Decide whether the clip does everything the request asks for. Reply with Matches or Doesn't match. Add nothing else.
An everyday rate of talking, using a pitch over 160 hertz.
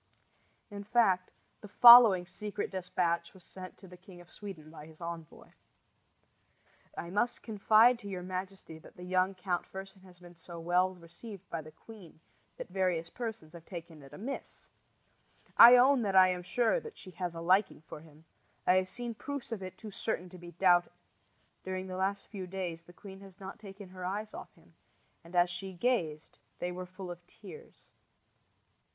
Matches